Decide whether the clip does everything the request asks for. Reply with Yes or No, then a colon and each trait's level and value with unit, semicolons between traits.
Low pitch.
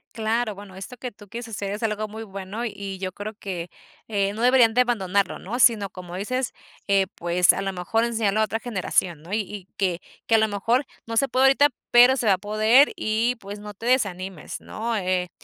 No: high, 210 Hz